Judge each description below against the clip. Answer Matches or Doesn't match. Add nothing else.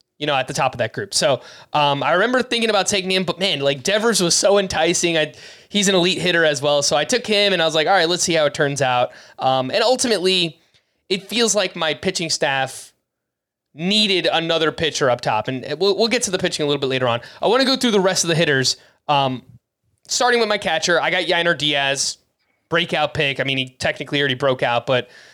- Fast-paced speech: Matches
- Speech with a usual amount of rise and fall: Doesn't match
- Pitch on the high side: Doesn't match